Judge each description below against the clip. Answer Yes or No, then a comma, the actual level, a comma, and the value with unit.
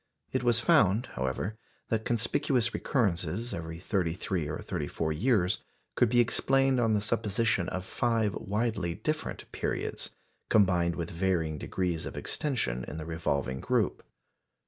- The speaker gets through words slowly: No, average, 145 wpm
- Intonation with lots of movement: Yes, wide, 5.7 semitones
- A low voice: Yes, very low, 95 Hz